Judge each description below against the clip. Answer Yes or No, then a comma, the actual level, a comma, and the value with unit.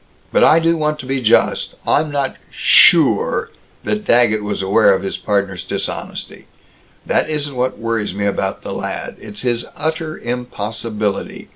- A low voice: Yes, low, 120 Hz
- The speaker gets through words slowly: No, average, 155 wpm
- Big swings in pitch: Yes, wide, 6.4 semitones